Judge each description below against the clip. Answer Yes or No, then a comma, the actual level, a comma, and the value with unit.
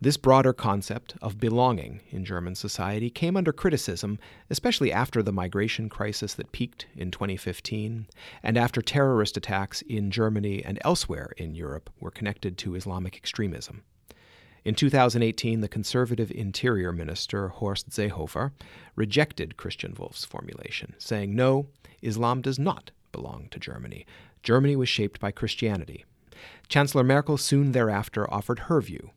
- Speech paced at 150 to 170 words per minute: No, average, 140 wpm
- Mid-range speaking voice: No, low, 110 Hz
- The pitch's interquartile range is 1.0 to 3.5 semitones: No, average, 4.0 semitones